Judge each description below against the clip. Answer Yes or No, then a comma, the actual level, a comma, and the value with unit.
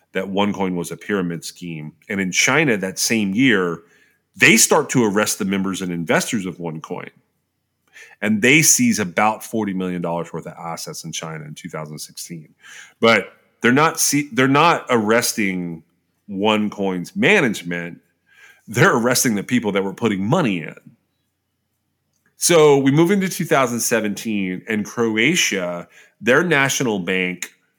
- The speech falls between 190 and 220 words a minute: No, slow, 135 wpm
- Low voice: Yes, very low, 95 Hz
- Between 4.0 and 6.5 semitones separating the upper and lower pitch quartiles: Yes, average, 4.9 semitones